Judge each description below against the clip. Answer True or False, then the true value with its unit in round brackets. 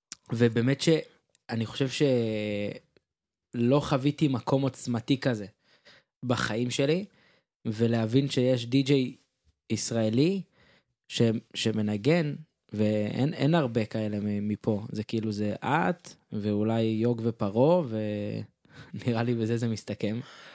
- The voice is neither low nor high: False (115 Hz)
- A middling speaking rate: False (90 wpm)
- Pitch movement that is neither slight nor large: True (4.2 semitones)